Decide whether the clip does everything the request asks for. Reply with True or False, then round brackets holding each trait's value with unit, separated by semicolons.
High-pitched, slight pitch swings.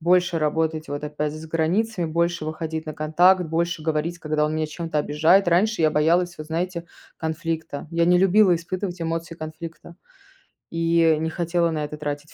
False (165 Hz; 1.8 semitones)